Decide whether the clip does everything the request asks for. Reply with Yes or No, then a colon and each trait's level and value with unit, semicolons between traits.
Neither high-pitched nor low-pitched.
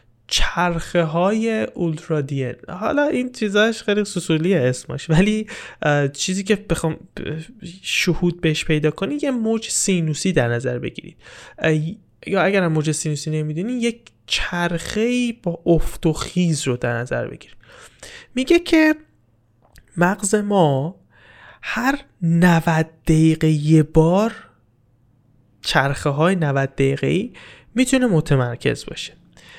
Yes: medium, 170 Hz